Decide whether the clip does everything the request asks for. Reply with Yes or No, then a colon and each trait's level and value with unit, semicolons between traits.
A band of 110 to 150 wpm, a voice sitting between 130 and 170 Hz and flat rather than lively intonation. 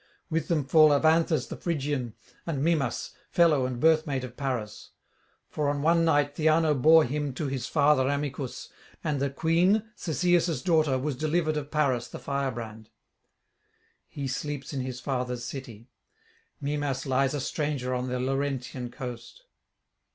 No: average, 145 wpm; medium, 140 Hz; average, 3.2 semitones